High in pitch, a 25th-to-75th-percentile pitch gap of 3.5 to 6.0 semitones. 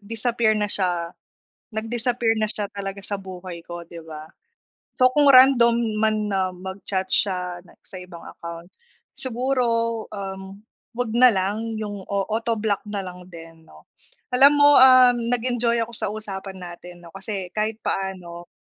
Yes: high, 200 Hz; average, 4.1 semitones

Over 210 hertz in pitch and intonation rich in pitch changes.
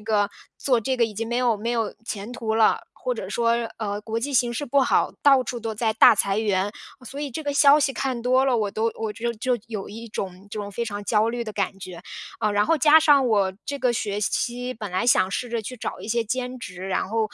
No: high, 230 Hz; average, 3.2 semitones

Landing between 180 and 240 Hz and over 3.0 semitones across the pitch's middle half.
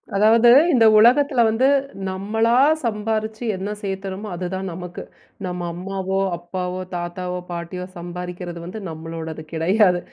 Yes: high, 190 Hz; average, 3.6 semitones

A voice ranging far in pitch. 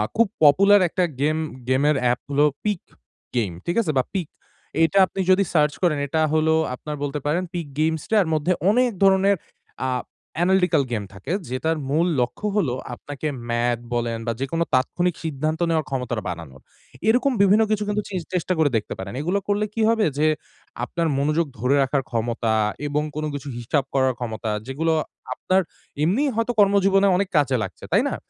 Yes: wide, 6.5 semitones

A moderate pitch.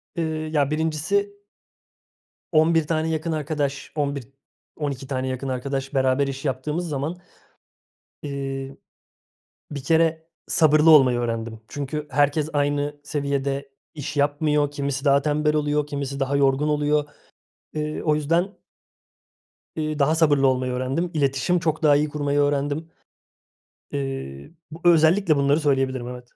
Yes: medium, 145 Hz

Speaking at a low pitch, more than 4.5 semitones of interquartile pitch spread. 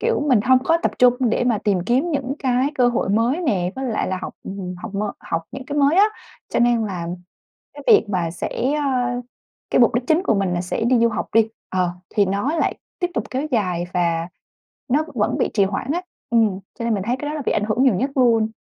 No: high, 240 Hz; average, 5.0 semitones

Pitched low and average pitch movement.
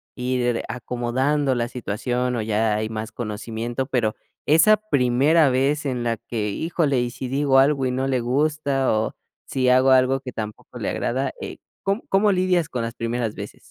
Yes: low, 125 Hz; average, 3.1 semitones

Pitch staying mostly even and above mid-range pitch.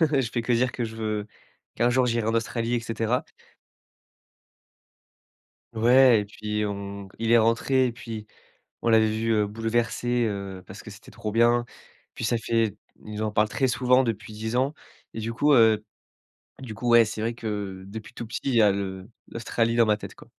No: narrow, 2.0 semitones; low, 115 Hz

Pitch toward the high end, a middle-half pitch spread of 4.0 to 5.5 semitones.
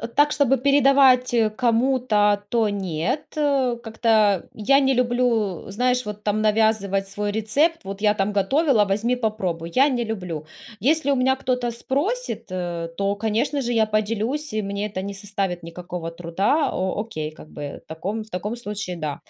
Yes: high, 215 Hz; average, 4.4 semitones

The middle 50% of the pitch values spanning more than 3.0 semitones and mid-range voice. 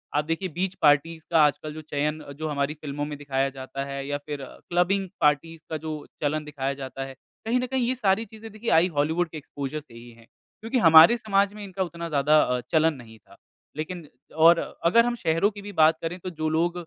Yes: average, 4.2 semitones; medium, 155 Hz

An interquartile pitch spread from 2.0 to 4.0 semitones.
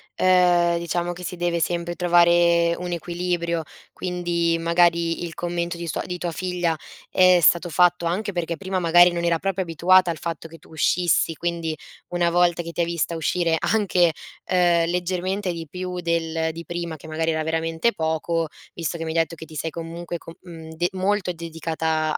No: narrow, 1.2 semitones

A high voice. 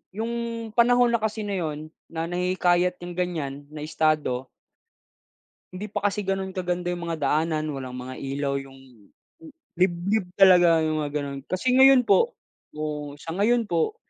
No: medium, 175 Hz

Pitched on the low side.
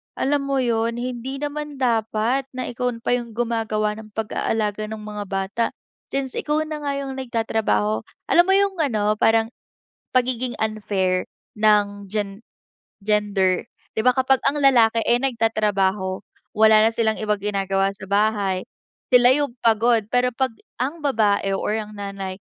No: high, 225 Hz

